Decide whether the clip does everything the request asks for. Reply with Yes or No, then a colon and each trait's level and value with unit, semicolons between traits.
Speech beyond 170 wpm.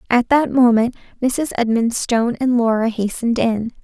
No: average, 140 wpm